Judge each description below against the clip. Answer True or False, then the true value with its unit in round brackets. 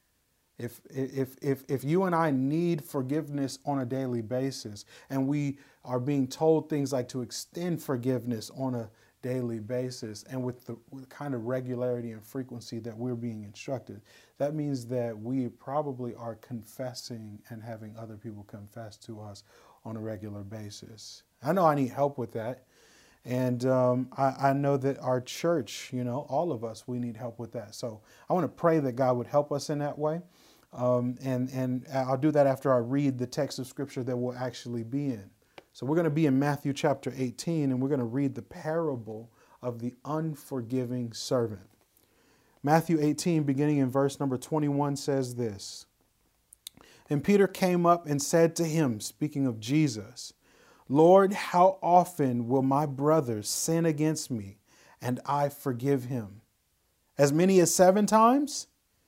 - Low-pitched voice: True (130 Hz)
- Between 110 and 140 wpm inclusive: False (175 wpm)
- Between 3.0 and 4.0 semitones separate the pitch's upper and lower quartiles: True (3.6 semitones)